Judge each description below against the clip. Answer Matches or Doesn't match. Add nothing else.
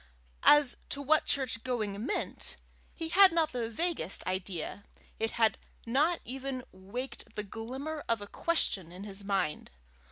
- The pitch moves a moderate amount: Doesn't match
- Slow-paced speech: Doesn't match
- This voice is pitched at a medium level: Doesn't match